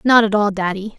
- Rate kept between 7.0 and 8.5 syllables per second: No, 5.6 syllables/s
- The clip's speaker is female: Yes, female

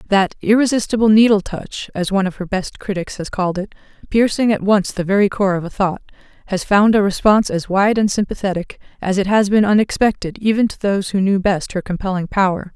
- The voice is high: Yes, high, 200 Hz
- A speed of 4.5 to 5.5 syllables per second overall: No, 5.9 syllables/s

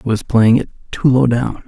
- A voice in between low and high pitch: No, low, 120 Hz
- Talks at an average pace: No, fast, 250 wpm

